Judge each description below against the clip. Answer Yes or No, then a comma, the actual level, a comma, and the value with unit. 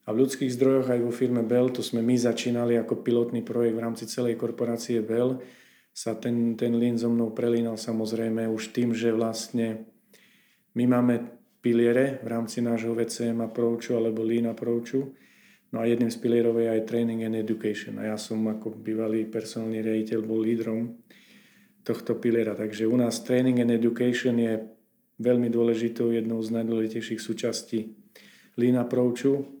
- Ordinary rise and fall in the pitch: No, narrow, 1.4 semitones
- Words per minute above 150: Yes, fast, 165 wpm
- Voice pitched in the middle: No, low, 115 Hz